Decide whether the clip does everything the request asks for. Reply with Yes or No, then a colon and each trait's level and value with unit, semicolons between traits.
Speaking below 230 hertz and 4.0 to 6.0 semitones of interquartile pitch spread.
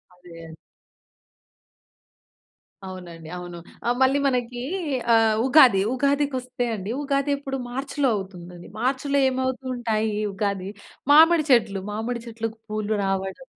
No: high, 235 Hz; wide, 5.5 semitones